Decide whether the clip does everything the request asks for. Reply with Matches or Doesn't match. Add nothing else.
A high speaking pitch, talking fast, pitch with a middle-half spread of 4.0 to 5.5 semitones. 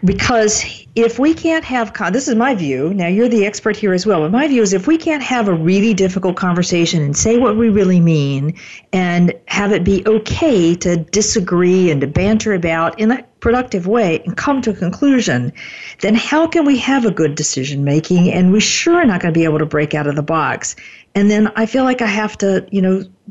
Matches